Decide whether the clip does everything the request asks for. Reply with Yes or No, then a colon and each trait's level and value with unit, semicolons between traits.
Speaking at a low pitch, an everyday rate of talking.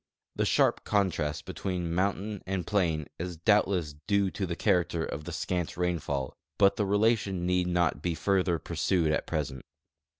Yes: very low, 90 Hz; average, 160 wpm